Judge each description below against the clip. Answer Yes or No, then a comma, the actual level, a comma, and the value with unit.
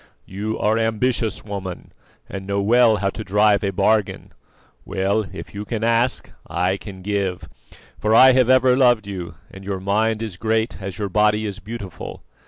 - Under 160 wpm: No, average, 175 wpm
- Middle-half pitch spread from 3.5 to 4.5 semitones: No, narrow, 2.4 semitones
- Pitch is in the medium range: No, low, 105 Hz